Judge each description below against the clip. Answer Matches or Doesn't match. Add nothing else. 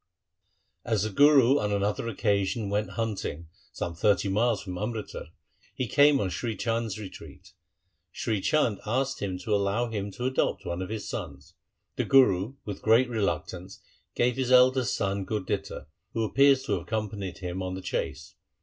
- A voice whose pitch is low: Matches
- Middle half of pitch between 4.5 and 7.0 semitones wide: Doesn't match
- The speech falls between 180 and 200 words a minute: Doesn't match